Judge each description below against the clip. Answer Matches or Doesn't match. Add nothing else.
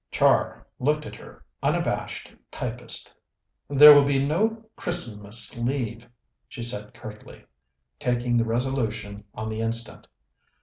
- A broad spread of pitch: Doesn't match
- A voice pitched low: Matches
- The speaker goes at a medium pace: Doesn't match